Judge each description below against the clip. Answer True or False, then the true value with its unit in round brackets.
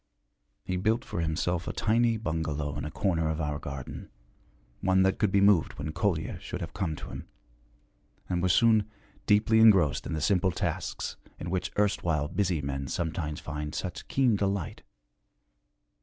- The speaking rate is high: False (165 wpm)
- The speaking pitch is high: False (90 Hz)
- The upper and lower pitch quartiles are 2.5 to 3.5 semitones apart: False (4.7 semitones)